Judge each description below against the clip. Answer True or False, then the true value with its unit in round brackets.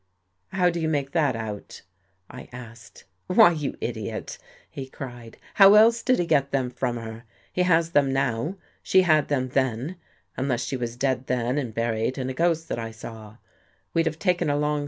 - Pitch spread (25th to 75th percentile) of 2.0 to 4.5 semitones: False (5.5 semitones)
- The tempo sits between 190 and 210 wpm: False (175 wpm)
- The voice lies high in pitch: False (130 Hz)